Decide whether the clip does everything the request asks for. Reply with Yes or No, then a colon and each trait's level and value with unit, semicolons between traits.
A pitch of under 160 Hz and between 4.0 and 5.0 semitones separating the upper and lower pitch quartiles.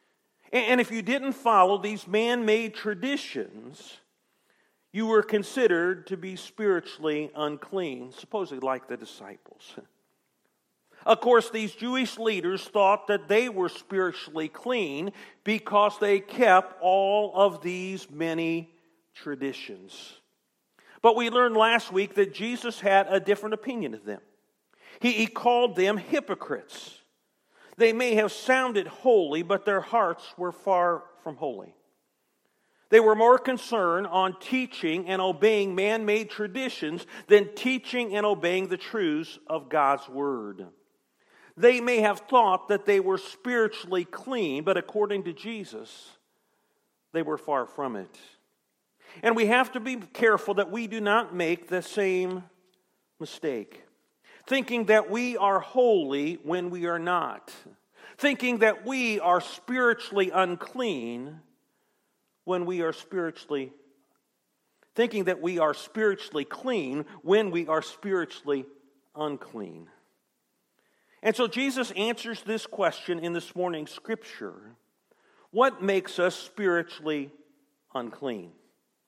No: high, 200 Hz; average, 4.5 semitones